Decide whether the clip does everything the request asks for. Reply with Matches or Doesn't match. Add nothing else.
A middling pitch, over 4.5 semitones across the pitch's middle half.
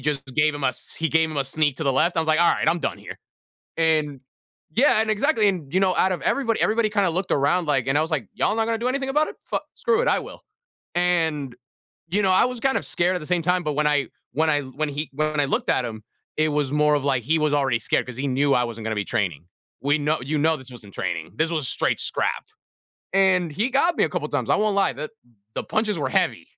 Matches